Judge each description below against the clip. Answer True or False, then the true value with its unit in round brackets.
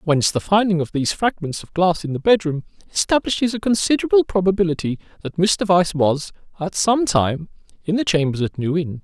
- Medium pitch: True (180 Hz)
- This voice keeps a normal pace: True (185 wpm)